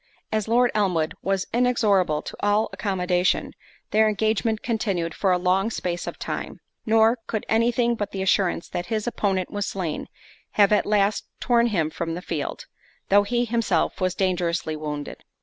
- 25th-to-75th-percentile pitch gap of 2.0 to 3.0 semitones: No, average, 3.6 semitones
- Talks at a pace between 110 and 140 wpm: No, average, 165 wpm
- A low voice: No, high, 200 Hz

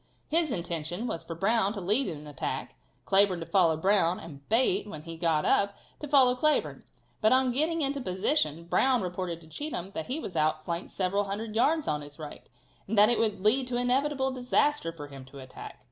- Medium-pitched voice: No, high, 200 Hz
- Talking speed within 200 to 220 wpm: Yes, fast, 205 wpm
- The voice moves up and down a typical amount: No, wide, 7.4 semitones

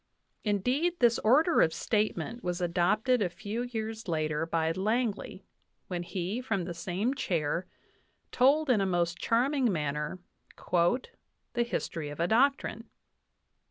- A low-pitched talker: No, high, 205 Hz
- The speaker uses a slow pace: Yes, slow, 130 wpm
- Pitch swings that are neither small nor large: No, wide, 5.8 semitones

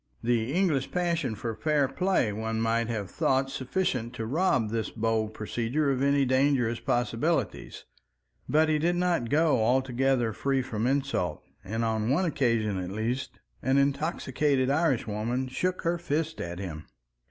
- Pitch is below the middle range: Yes, low, 130 Hz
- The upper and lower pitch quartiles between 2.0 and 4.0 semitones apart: No, average, 4.7 semitones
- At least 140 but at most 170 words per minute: Yes, average, 155 wpm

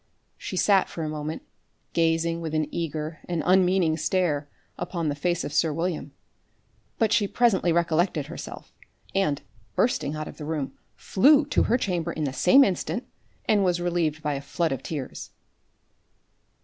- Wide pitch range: No, average, 3.2 semitones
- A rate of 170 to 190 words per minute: No, average, 160 wpm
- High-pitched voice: No, medium, 165 Hz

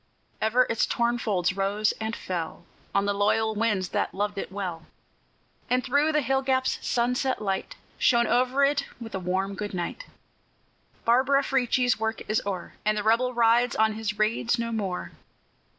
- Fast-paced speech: No, average, 165 wpm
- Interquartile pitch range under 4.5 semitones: Yes, average, 3.7 semitones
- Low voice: No, high, 225 Hz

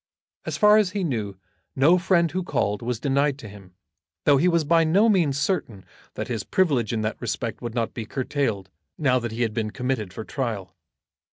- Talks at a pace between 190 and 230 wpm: Yes, average, 200 wpm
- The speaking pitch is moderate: No, low, 130 Hz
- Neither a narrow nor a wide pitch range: No, wide, 6.9 semitones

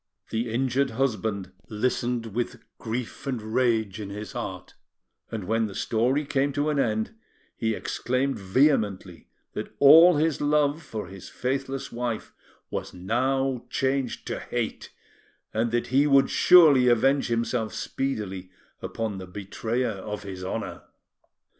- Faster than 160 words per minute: No, slow, 135 wpm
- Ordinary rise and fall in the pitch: Yes, average, 4.0 semitones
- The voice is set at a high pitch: No, low, 120 Hz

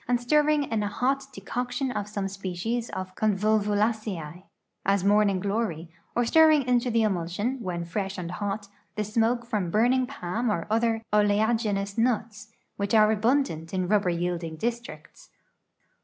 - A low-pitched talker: No, high, 210 Hz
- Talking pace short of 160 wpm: Yes, average, 140 wpm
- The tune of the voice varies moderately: Yes, average, 3.7 semitones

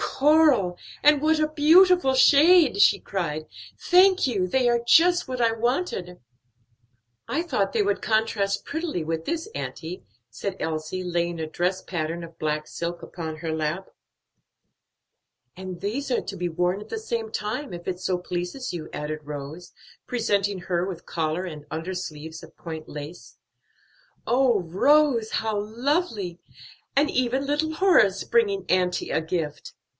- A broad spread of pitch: Yes, wide, 7.5 semitones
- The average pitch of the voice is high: Yes, high, 195 Hz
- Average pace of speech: Yes, average, 150 wpm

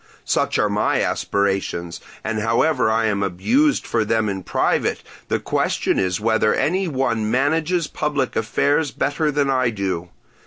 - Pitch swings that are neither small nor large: No, wide, 6.4 semitones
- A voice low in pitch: Yes, low, 115 Hz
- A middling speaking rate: Yes, average, 150 wpm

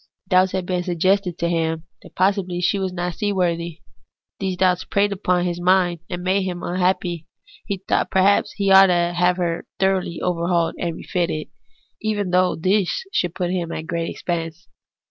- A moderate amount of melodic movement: No, narrow, 1.7 semitones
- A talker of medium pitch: Yes, medium, 180 Hz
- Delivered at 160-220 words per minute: Yes, average, 175 wpm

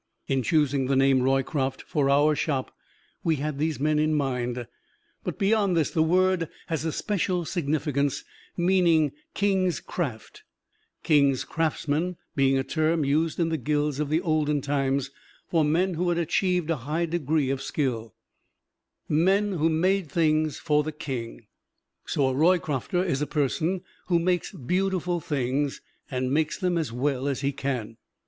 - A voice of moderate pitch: Yes, medium, 150 Hz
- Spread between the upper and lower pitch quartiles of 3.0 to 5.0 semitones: Yes, average, 3.7 semitones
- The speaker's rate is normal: Yes, average, 155 wpm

